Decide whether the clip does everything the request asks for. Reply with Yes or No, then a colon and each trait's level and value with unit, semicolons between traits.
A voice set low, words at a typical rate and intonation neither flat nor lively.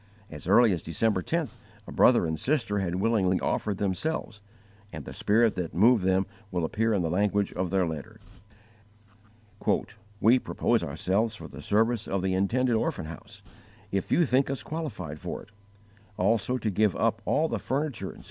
Yes: low, 105 Hz; average, 175 wpm; average, 4.0 semitones